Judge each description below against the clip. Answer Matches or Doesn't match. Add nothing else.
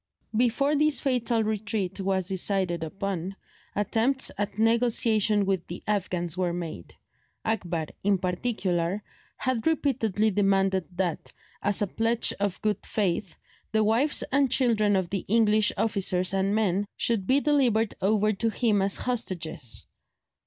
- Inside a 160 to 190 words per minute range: Doesn't match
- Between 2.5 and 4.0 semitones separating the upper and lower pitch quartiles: Matches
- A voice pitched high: Matches